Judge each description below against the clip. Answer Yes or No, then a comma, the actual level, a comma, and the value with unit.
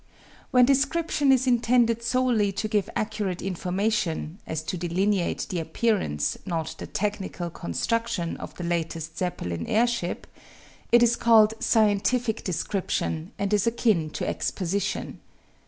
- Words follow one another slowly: Yes, slow, 125 wpm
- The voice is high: Yes, high, 205 Hz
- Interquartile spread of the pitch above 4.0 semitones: Yes, average, 5.0 semitones